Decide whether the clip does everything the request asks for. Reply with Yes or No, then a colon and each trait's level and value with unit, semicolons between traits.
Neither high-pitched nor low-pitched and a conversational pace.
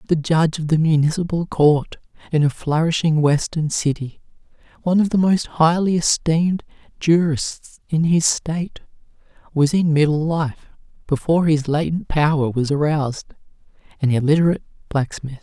No: medium, 155 Hz; slow, 130 wpm